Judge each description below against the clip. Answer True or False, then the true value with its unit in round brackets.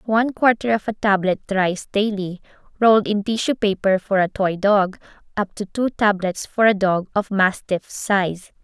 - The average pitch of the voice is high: True (205 Hz)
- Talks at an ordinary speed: True (175 wpm)